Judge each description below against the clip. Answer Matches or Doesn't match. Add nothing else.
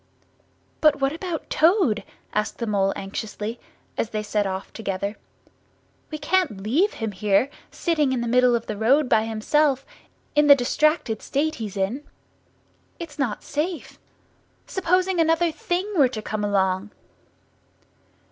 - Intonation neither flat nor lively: Doesn't match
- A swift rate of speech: Doesn't match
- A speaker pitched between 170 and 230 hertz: Doesn't match